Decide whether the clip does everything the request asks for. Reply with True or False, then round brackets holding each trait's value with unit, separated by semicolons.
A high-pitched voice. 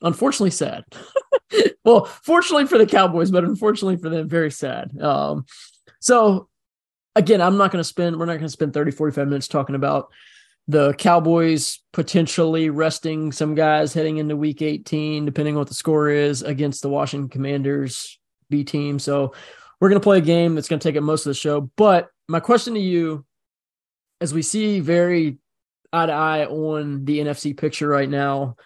False (155 Hz)